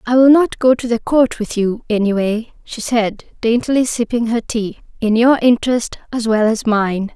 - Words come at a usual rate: Yes, average, 185 wpm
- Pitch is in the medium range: No, high, 230 Hz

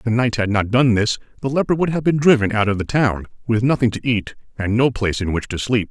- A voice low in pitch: Yes, low, 115 Hz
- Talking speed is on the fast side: Yes, fast, 285 wpm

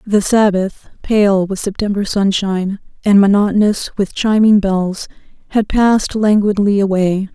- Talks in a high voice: Yes, high, 200 Hz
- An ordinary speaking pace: No, slow, 125 wpm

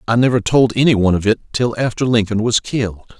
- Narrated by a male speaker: Yes, male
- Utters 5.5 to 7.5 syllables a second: Yes, 5.9 syllables/s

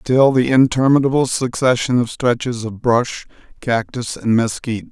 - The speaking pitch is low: Yes, low, 125 Hz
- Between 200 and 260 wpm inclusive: No, slow, 135 wpm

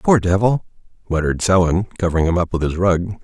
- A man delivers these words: Yes, male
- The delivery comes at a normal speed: Yes, average, 185 wpm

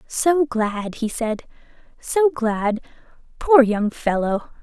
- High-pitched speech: Yes, high, 245 Hz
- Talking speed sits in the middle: No, slow, 115 wpm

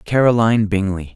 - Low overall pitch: Yes, low, 105 Hz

